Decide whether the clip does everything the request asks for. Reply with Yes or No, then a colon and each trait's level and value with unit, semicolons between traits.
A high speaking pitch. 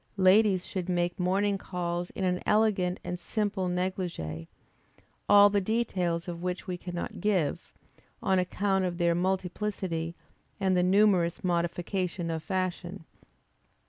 No: medium, 180 Hz